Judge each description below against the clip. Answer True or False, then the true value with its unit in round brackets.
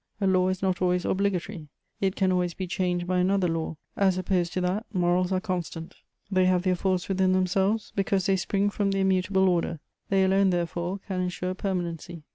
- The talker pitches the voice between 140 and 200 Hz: True (185 Hz)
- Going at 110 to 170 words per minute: False (195 wpm)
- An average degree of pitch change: False (1.4 semitones)